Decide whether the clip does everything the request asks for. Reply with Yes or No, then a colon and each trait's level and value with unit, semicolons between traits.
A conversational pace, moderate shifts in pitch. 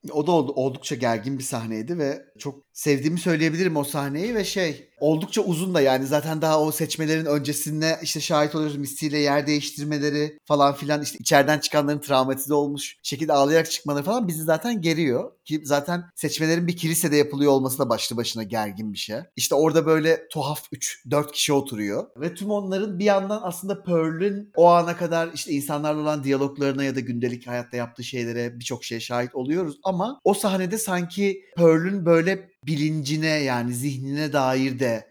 No: fast, 165 wpm; average, 3.1 semitones